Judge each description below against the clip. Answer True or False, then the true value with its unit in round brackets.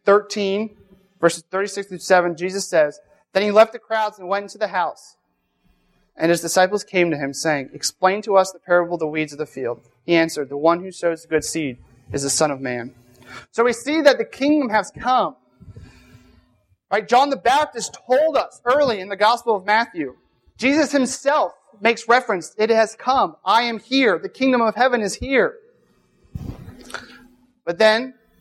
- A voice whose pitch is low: False (200 Hz)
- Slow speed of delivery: False (185 wpm)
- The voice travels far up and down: True (6.7 semitones)